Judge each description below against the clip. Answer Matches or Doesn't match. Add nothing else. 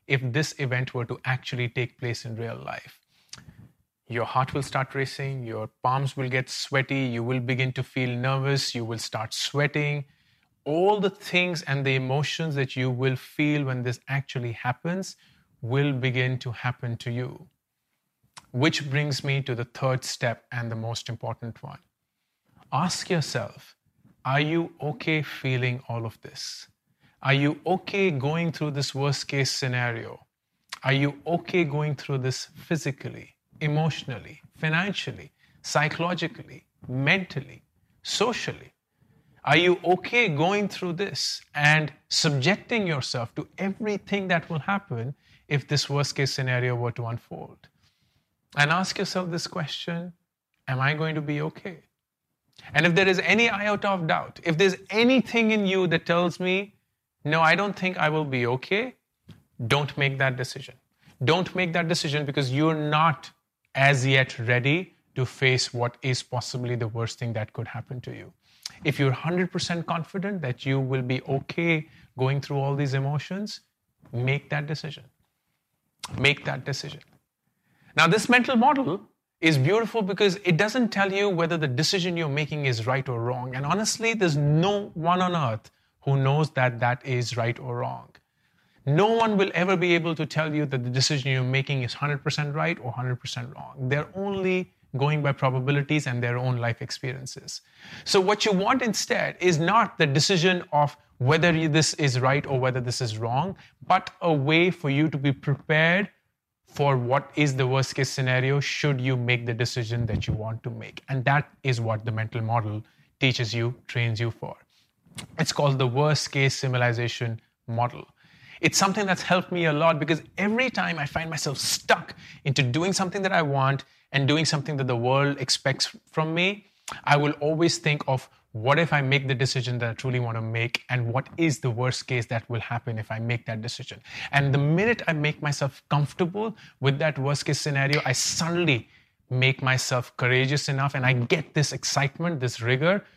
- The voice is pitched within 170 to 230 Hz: Doesn't match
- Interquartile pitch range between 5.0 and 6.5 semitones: Doesn't match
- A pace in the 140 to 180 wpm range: Matches